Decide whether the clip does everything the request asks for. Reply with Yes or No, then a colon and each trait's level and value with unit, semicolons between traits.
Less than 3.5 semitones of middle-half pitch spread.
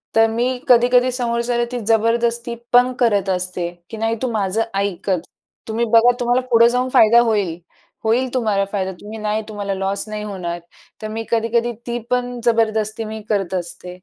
Yes: average, 2.8 semitones